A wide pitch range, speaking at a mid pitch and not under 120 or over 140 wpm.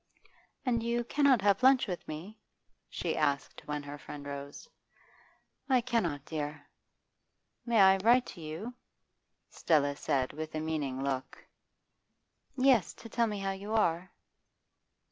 Yes: wide, 7.8 semitones; medium, 175 Hz; slow, 135 wpm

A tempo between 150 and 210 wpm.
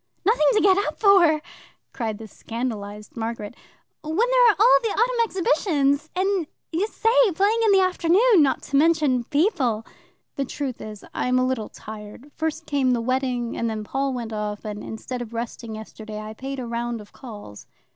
Yes: average, 180 wpm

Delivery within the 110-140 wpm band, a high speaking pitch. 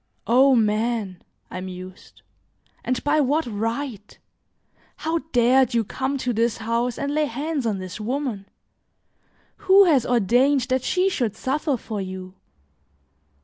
Yes: slow, 135 wpm; high, 245 Hz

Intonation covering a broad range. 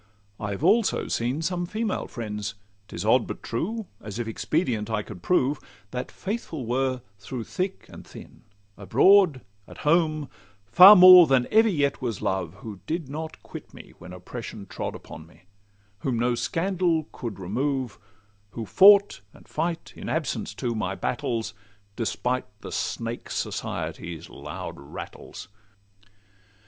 Yes: wide, 7.6 semitones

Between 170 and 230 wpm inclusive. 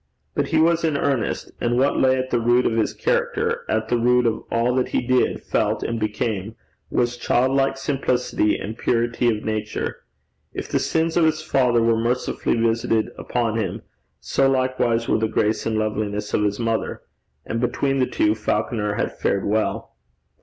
Yes: average, 180 wpm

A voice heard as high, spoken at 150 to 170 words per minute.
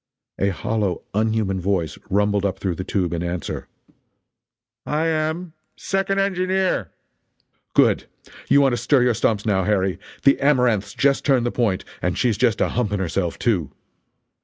No: low, 110 Hz; average, 155 wpm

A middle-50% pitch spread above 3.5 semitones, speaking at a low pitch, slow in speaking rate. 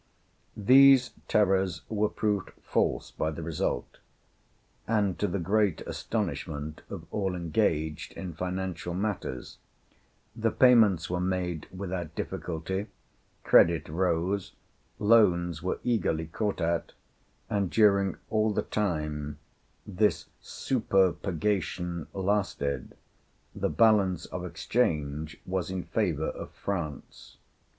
Yes: average, 3.9 semitones; very low, 95 Hz; slow, 105 wpm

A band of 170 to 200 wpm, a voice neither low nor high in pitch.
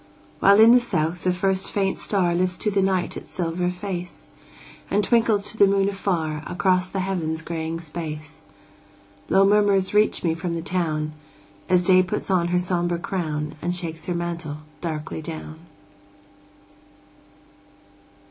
No: average, 150 wpm; medium, 180 Hz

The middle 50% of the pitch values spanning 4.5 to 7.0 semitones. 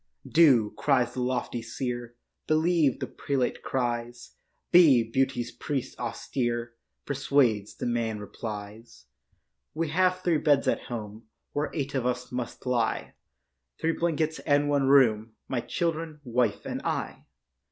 No: average, 3.7 semitones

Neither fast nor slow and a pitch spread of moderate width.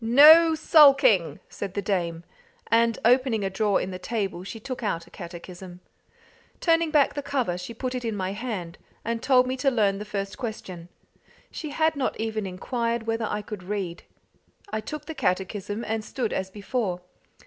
Yes: average, 180 wpm; average, 5.0 semitones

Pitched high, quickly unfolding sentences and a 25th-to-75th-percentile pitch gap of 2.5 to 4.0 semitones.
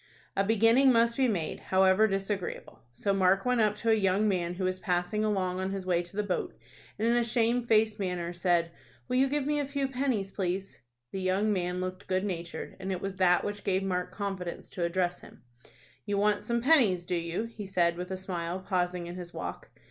Yes: high, 195 Hz; fast, 215 wpm; average, 3.2 semitones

